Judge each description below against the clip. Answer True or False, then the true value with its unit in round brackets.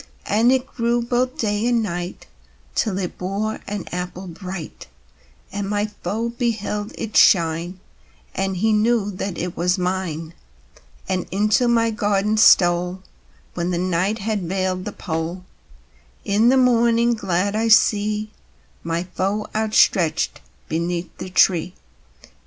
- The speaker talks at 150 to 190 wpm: False (135 wpm)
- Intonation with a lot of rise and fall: False (3.4 semitones)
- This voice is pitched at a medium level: False (200 Hz)